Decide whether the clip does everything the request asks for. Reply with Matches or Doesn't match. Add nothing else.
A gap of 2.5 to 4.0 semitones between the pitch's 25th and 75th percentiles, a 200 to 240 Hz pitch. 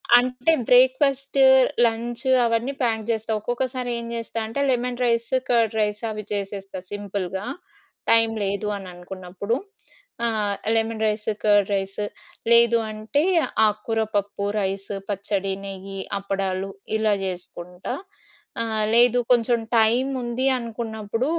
Matches